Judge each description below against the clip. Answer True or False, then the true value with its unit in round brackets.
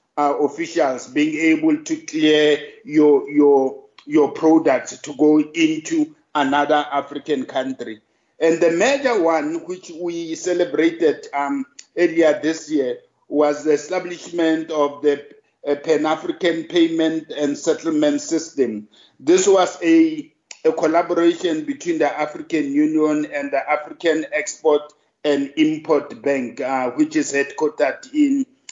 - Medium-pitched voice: True (155 Hz)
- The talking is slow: True (125 wpm)